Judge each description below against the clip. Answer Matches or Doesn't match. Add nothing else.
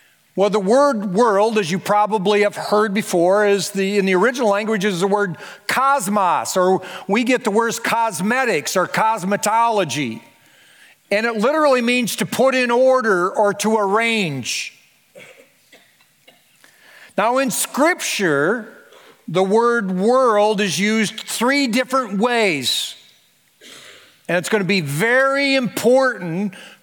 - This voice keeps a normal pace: Doesn't match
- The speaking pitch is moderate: Doesn't match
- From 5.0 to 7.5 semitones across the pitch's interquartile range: Doesn't match